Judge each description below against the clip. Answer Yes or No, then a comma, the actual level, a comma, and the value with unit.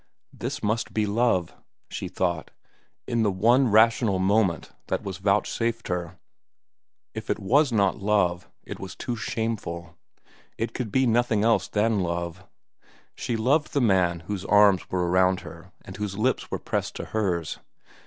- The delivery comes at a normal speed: Yes, average, 155 wpm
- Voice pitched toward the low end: Yes, low, 105 Hz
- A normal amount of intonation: Yes, average, 3.7 semitones